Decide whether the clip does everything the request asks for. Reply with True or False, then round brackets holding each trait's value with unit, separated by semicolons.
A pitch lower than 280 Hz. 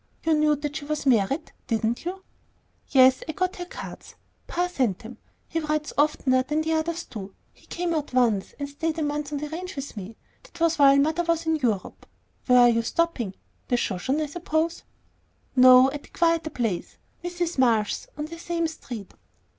False (295 Hz)